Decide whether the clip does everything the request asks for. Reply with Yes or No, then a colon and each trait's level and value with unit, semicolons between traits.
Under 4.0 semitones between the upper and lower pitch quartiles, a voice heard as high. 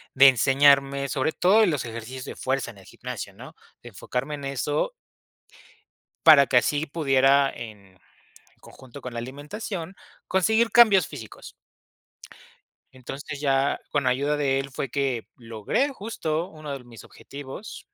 No: average, 3.1 semitones; medium, 140 Hz